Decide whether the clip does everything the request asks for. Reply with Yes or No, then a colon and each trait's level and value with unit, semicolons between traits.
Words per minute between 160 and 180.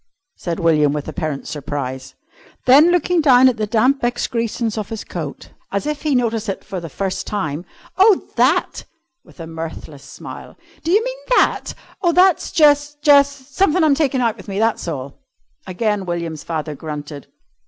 Yes: average, 170 wpm